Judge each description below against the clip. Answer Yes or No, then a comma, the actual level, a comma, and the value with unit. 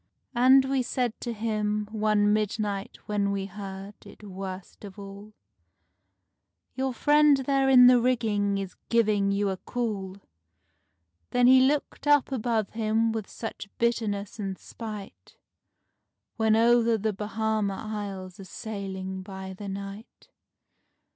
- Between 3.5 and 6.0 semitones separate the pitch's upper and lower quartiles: No, average, 2.9 semitones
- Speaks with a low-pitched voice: No, high, 215 Hz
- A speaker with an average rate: No, slow, 130 wpm